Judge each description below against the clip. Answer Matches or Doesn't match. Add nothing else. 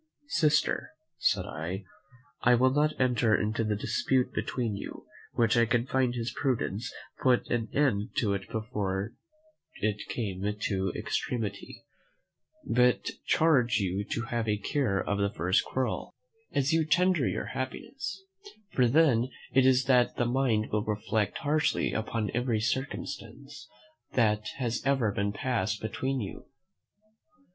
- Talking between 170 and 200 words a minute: Doesn't match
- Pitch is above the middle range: Doesn't match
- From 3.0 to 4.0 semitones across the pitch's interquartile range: Matches